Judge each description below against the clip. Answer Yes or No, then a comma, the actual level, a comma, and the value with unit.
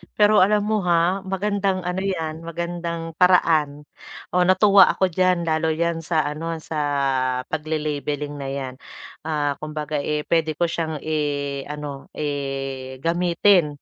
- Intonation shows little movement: No, average, 3.3 semitones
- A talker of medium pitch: Yes, medium, 160 Hz